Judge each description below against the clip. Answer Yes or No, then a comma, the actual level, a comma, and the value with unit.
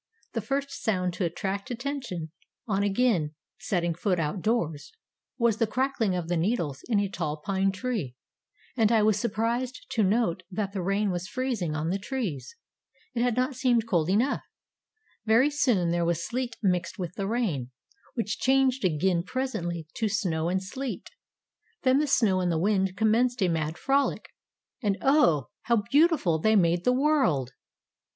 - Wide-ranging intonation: Yes, wide, 6.0 semitones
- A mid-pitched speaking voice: No, high, 205 Hz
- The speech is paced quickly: No, average, 165 wpm